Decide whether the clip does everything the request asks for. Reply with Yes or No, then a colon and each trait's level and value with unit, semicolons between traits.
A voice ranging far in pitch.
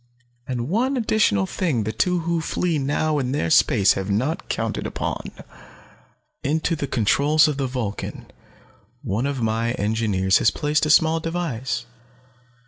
Yes: wide, 6.2 semitones